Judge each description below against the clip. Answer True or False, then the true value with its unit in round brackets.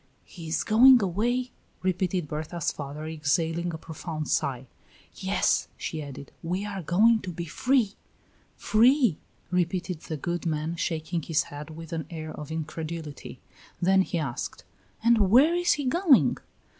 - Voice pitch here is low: False (170 Hz)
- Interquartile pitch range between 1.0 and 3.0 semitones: False (4.7 semitones)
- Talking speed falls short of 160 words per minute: True (145 wpm)